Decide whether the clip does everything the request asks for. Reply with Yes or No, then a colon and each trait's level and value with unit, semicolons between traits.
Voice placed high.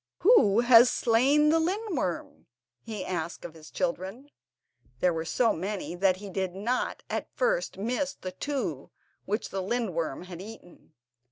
Yes: high, 205 Hz